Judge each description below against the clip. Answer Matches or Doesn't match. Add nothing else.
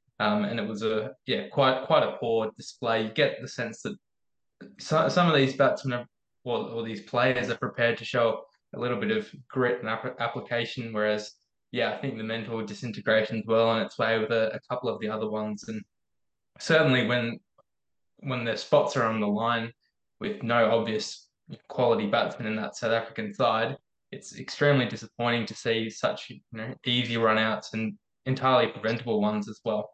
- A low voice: Matches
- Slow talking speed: Doesn't match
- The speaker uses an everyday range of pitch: Doesn't match